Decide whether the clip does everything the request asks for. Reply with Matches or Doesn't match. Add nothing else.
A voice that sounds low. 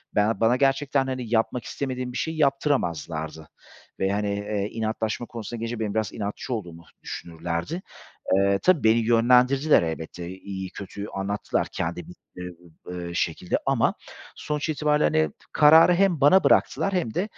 Matches